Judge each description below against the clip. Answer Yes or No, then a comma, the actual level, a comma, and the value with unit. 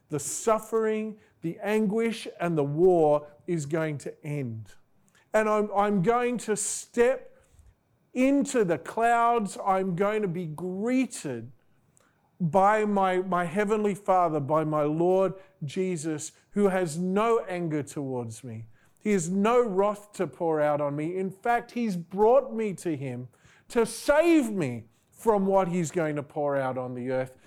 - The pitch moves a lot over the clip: Yes, wide, 6.2 semitones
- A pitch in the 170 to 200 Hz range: Yes, medium, 185 Hz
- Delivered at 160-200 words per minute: No, average, 150 wpm